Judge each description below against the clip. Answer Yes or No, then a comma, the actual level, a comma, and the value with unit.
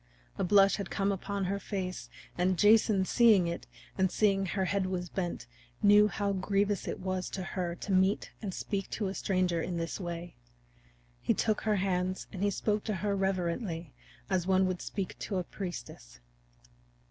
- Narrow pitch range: Yes, narrow, 1.9 semitones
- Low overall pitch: No, high, 190 Hz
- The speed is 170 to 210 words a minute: Yes, average, 180 wpm